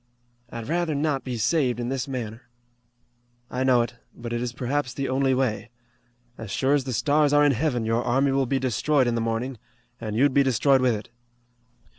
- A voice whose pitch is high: No, low, 130 Hz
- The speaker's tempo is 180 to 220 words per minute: Yes, average, 200 wpm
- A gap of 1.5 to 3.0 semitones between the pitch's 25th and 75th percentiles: Yes, average, 2.7 semitones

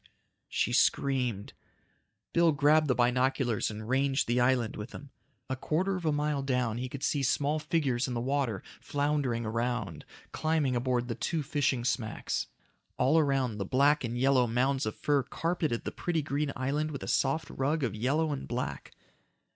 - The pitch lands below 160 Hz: Yes, low, 135 Hz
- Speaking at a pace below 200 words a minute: Yes, average, 170 wpm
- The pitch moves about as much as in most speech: Yes, average, 3.2 semitones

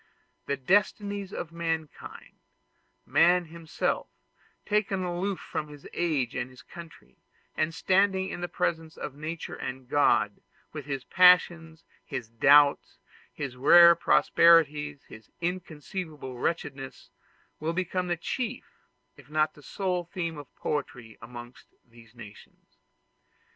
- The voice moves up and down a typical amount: Yes, average, 4.0 semitones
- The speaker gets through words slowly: Yes, slow, 125 wpm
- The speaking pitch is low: No, medium, 160 Hz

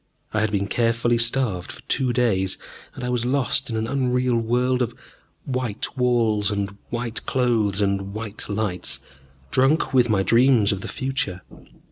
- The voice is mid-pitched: No, low, 115 Hz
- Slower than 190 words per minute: Yes, average, 160 wpm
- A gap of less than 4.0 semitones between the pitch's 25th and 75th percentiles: Yes, average, 3.4 semitones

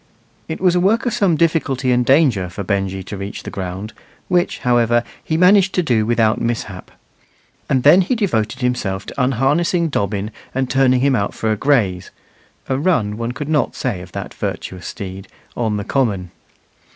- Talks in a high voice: No, low, 125 Hz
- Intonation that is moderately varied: No, wide, 7.1 semitones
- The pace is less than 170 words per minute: No, average, 180 wpm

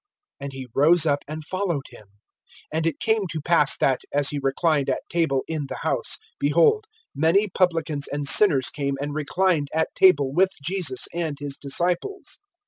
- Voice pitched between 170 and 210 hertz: No, medium, 155 Hz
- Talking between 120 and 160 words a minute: No, average, 170 wpm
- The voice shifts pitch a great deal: No, average, 3.7 semitones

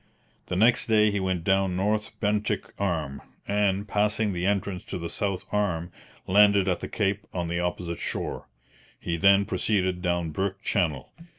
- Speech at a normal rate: Yes, average, 165 wpm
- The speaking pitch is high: No, very low, 95 Hz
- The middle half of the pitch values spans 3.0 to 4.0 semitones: No, narrow, 2.6 semitones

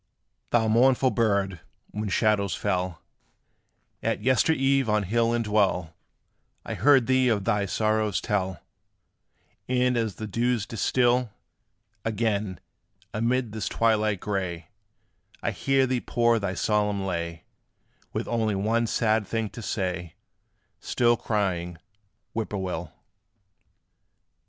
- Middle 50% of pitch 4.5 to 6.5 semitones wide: No, average, 3.3 semitones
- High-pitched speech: No, low, 110 Hz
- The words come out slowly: Yes, slow, 120 wpm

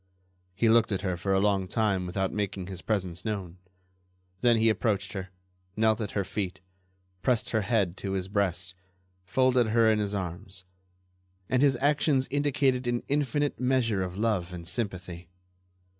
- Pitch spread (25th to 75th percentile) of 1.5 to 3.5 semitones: No, average, 4.1 semitones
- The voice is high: No, low, 105 Hz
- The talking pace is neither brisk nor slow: Yes, average, 160 wpm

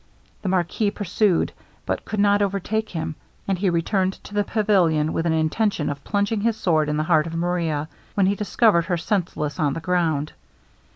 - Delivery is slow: No, average, 185 wpm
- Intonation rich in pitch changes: No, average, 4.1 semitones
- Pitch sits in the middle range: Yes, medium, 180 Hz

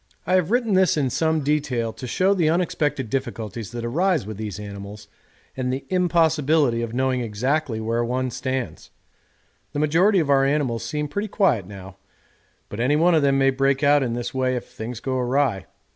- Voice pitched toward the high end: No, low, 135 Hz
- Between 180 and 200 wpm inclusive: Yes, average, 190 wpm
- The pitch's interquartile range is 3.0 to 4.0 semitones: No, average, 4.9 semitones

